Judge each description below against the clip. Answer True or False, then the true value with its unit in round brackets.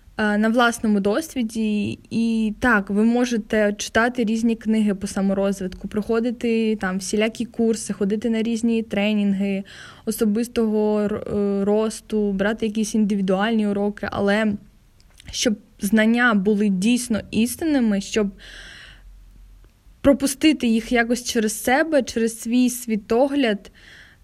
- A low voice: False (220 Hz)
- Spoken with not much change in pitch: True (2.2 semitones)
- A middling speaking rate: False (100 wpm)